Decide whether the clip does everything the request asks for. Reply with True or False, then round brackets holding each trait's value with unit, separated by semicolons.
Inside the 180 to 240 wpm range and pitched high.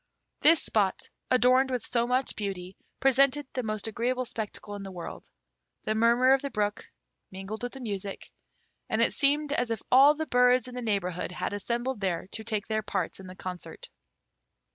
True (185 wpm; 230 Hz)